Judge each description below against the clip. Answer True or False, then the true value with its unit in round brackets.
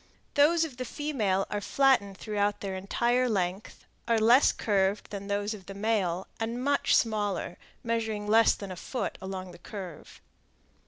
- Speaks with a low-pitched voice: False (210 Hz)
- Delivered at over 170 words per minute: False (160 wpm)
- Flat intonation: False (3.4 semitones)